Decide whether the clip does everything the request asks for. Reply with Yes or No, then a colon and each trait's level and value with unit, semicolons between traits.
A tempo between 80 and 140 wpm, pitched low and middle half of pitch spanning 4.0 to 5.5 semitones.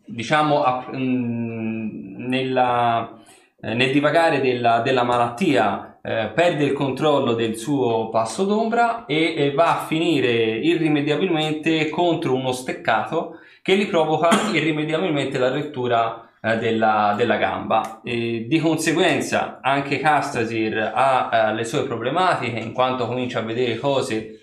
Yes: average, 130 wpm; low, 130 Hz; average, 5.2 semitones